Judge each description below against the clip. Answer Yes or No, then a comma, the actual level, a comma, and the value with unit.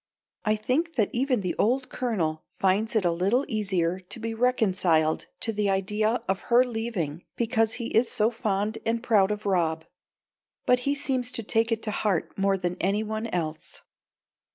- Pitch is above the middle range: Yes, high, 215 Hz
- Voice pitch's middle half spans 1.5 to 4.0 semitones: Yes, average, 3.6 semitones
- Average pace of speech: Yes, average, 175 wpm